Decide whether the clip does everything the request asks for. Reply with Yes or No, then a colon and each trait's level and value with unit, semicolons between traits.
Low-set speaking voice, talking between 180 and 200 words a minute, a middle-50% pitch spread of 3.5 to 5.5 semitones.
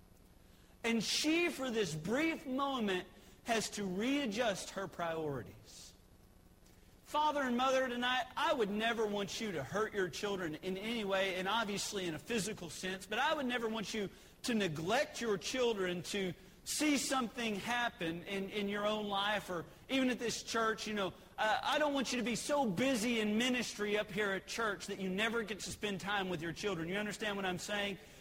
No: high, 210 Hz; average, 190 wpm; average, 4.2 semitones